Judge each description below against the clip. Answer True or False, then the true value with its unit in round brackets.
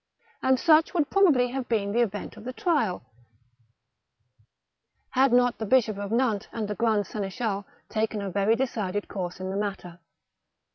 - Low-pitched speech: False (220 Hz)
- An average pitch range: True (3.9 semitones)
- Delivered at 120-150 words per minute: False (160 wpm)